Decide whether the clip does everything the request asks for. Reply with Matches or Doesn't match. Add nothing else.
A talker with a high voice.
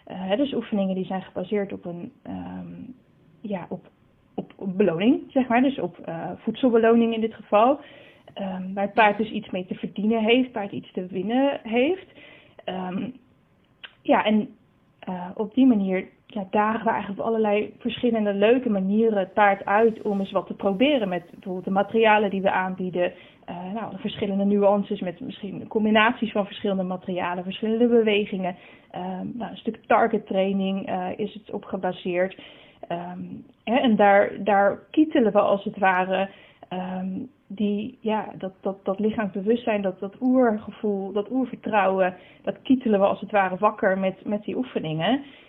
Matches